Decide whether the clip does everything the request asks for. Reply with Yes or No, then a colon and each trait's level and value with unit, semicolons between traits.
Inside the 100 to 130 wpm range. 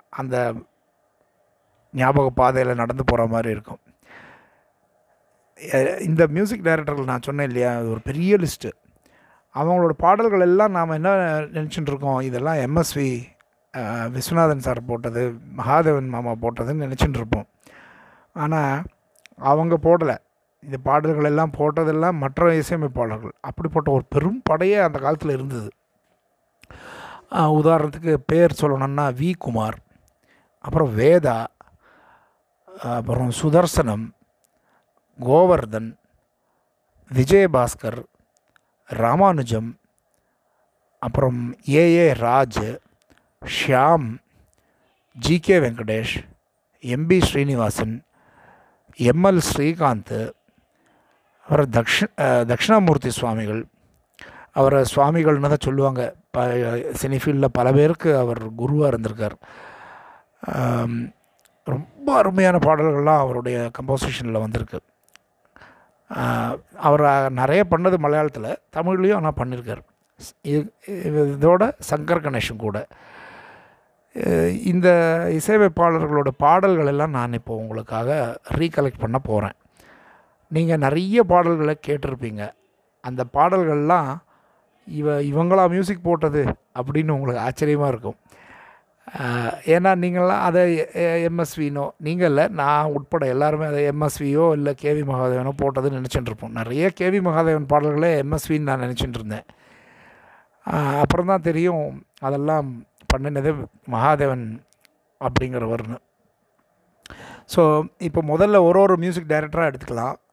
No: average, 90 wpm